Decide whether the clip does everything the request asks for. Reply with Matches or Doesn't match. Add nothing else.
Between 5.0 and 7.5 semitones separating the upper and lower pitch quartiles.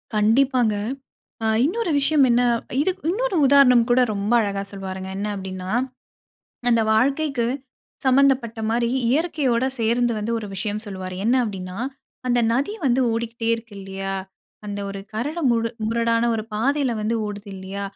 Doesn't match